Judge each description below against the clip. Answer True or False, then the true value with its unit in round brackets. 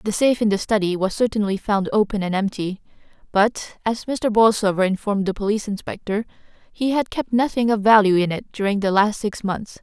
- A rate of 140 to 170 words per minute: False (195 wpm)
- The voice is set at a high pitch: True (210 Hz)